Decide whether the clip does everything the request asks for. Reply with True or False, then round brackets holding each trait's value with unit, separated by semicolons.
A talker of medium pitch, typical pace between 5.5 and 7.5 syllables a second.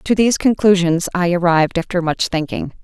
True (180 Hz; 5.6 syllables/s)